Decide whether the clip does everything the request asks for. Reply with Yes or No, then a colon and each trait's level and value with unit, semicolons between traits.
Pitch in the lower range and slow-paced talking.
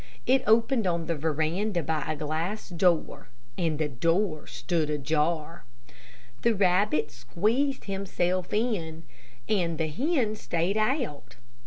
No: medium, 175 Hz; slow, 125 wpm